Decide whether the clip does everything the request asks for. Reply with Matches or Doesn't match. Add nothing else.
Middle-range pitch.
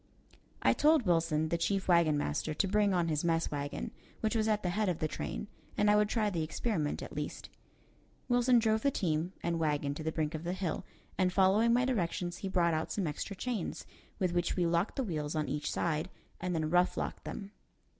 Matches